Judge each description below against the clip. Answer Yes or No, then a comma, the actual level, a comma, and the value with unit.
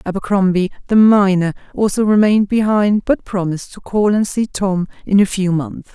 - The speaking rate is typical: Yes, average, 170 wpm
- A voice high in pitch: Yes, high, 200 Hz